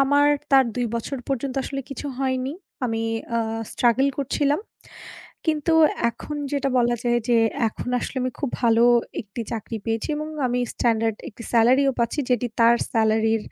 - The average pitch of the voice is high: Yes, high, 245 Hz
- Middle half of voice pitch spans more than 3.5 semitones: No, average, 3.1 semitones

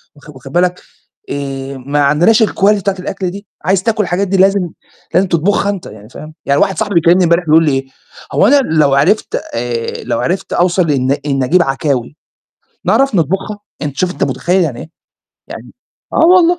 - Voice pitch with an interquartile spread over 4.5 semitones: Yes, wide, 5.6 semitones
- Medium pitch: Yes, medium, 175 Hz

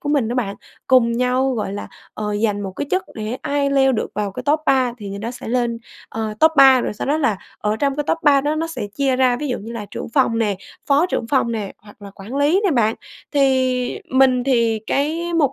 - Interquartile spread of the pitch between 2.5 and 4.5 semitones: Yes, average, 4.1 semitones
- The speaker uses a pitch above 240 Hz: Yes, very high, 250 Hz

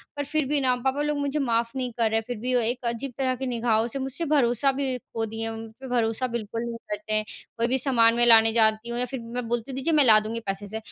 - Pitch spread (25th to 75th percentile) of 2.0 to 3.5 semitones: Yes, average, 2.8 semitones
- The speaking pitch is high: Yes, high, 240 Hz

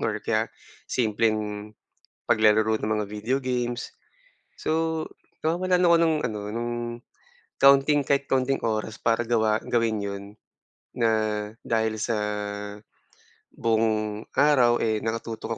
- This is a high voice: No, low, 115 Hz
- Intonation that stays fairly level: No, average, 3.7 semitones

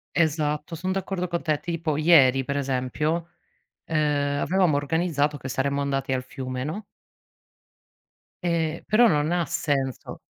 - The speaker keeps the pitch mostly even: No, average, 3.2 semitones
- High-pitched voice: No, medium, 150 Hz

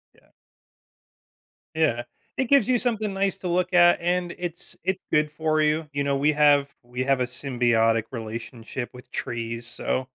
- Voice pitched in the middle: Yes, medium, 150 Hz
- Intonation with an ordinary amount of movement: No, wide, 6.2 semitones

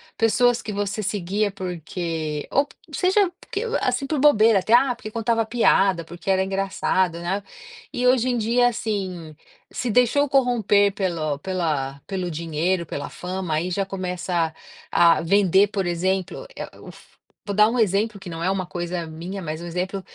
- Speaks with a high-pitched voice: Yes, high, 195 Hz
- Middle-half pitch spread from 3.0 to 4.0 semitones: No, average, 4.5 semitones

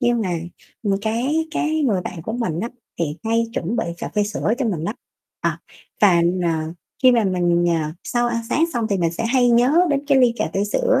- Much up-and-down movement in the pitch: Yes, wide, 5.7 semitones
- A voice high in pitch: Yes, high, 225 Hz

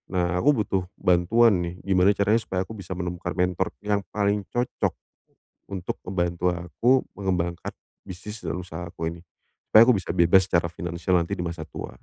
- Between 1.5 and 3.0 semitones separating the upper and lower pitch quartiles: Yes, average, 2.7 semitones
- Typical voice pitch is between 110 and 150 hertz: No, very low, 90 Hz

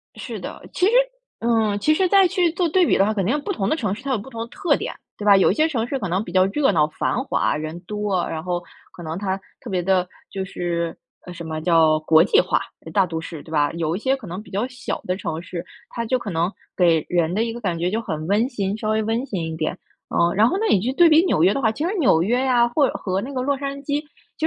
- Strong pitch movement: Yes, wide, 6.9 semitones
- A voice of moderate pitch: No, high, 205 Hz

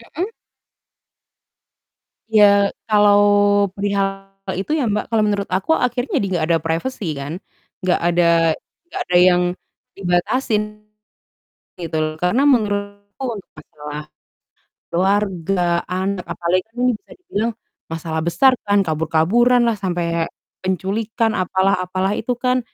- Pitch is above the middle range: Yes, high, 195 Hz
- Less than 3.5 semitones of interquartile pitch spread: No, average, 3.8 semitones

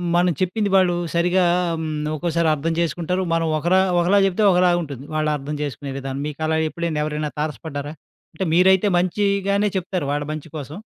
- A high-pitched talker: No, medium, 170 Hz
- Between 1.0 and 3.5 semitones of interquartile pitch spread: Yes, average, 3.2 semitones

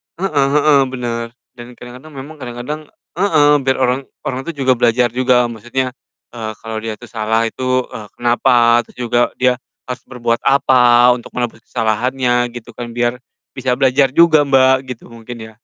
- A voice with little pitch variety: Yes, narrow, 1.9 semitones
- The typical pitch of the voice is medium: No, low, 125 Hz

